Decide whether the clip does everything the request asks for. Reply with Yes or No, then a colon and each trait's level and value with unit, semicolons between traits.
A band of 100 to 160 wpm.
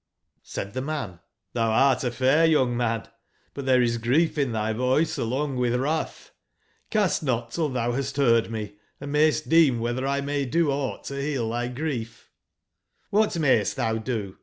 No: average, 185 wpm